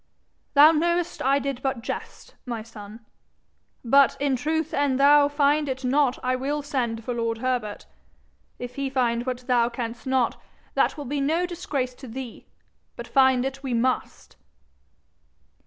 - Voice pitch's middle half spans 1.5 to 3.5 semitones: Yes, average, 2.8 semitones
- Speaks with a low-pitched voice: No, very high, 260 Hz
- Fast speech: No, average, 155 wpm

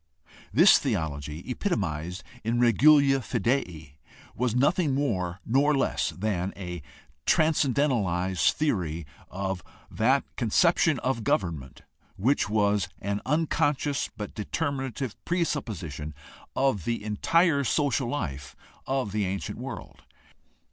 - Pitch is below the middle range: Yes, low, 115 Hz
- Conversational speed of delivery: No, slow, 105 wpm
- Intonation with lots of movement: Yes, wide, 7.4 semitones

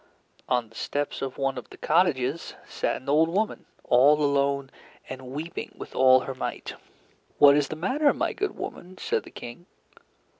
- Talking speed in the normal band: Yes, average, 175 wpm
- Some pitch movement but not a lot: Yes, average, 3.9 semitones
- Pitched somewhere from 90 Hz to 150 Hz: Yes, medium, 140 Hz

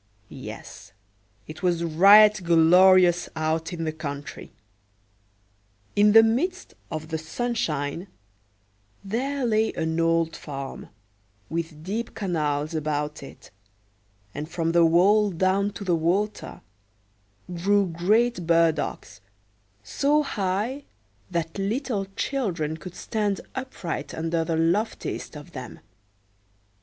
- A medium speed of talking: No, slow, 110 wpm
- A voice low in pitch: No, medium, 175 Hz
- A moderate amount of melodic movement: Yes, average, 4.5 semitones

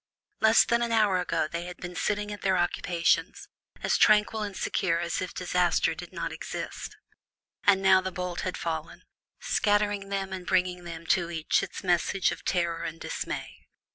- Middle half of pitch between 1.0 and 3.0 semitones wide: Yes, average, 2.7 semitones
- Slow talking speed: No, average, 170 wpm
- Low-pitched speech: No, medium, 185 Hz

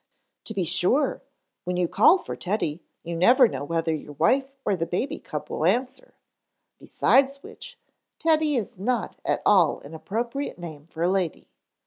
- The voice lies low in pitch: No, high, 190 Hz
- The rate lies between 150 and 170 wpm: Yes, average, 165 wpm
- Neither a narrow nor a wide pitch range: No, wide, 7.6 semitones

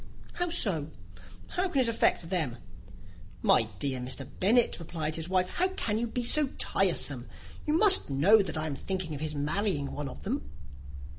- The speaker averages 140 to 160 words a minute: No, average, 175 wpm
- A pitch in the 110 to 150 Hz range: No, medium, 180 Hz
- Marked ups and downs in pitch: Yes, wide, 8.0 semitones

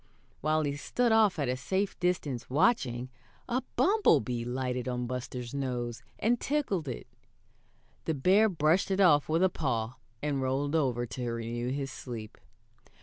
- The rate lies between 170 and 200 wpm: No, average, 150 wpm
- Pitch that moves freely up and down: Yes, wide, 6.5 semitones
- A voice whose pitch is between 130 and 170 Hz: Yes, medium, 140 Hz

